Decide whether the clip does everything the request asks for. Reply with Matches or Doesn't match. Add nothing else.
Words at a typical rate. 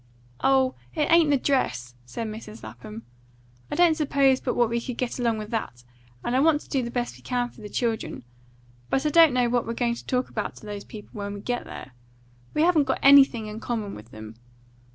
Doesn't match